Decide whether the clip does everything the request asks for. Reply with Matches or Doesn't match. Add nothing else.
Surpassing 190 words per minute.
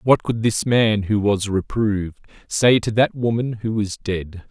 Doesn't match